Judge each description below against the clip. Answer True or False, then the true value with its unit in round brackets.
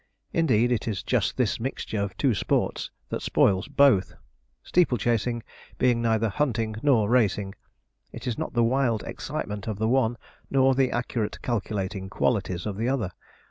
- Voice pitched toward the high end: False (115 Hz)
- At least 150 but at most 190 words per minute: True (160 wpm)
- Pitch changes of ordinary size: True (3.5 semitones)